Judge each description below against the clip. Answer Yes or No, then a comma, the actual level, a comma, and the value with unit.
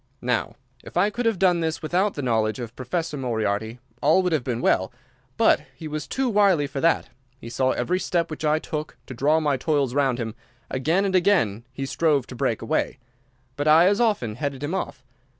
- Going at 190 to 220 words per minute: Yes, fast, 205 wpm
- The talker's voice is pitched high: No, medium, 150 Hz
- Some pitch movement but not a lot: No, wide, 5.7 semitones